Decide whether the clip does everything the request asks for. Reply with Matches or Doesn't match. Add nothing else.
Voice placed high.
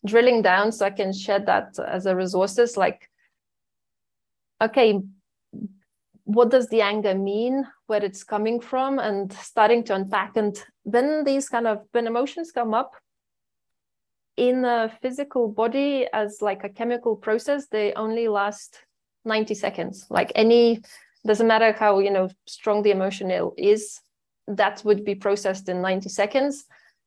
Matches